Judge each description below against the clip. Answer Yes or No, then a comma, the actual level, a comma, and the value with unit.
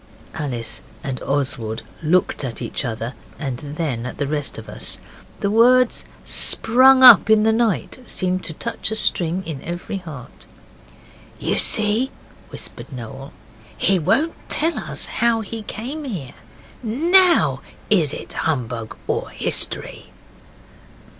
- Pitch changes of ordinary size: No, wide, 8.8 semitones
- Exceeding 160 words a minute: No, slow, 135 wpm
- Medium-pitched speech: Yes, medium, 180 Hz